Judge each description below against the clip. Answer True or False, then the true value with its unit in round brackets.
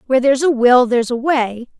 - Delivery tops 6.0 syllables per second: True (6.4 syllables/s)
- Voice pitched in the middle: False (255 Hz)